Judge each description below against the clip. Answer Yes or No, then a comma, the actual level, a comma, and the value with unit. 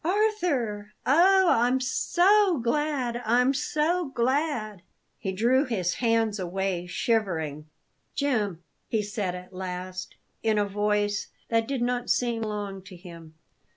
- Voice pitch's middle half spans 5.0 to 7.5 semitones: Yes, wide, 5.5 semitones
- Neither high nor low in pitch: No, high, 225 Hz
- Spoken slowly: Yes, slow, 130 wpm